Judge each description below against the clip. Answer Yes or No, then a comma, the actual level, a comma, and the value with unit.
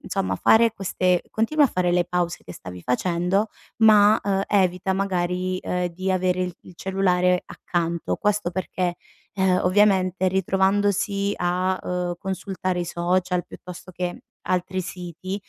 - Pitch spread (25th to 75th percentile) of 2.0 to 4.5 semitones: No, narrow, 1.4 semitones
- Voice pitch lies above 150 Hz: Yes, medium, 185 Hz